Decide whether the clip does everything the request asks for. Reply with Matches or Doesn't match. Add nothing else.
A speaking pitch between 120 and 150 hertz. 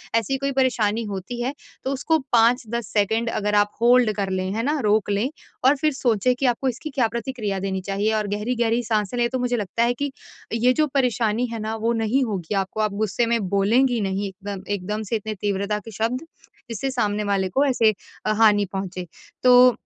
Doesn't match